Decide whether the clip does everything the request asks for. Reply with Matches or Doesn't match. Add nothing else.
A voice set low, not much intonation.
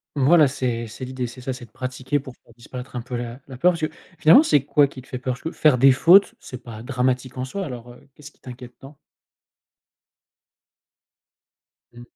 Matches